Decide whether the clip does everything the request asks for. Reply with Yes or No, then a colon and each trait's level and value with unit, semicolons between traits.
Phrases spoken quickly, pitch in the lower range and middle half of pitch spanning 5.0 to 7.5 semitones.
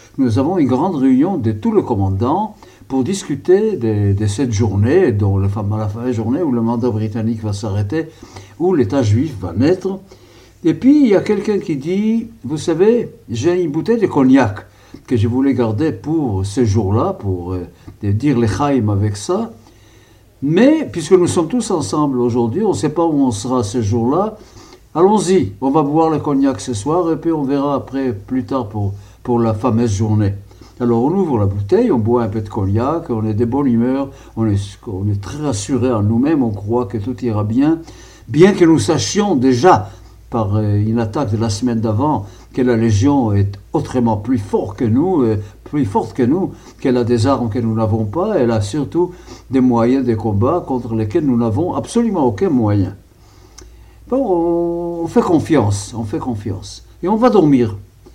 No: average, 195 wpm; low, 120 Hz; wide, 5.6 semitones